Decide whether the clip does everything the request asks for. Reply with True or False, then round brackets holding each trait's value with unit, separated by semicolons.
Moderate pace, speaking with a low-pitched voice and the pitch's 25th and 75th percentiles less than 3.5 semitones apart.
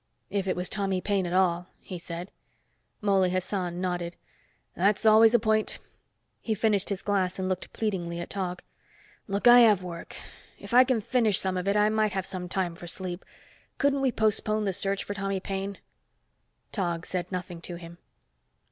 False (180 wpm; 195 Hz; 2.8 semitones)